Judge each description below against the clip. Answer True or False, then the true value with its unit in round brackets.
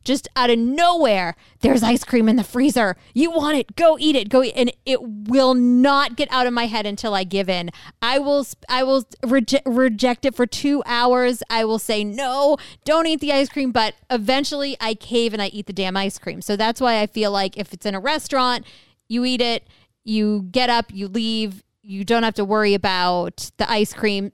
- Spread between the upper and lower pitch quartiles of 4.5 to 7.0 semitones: False (4.0 semitones)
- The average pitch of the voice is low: False (240 Hz)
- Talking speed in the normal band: False (220 wpm)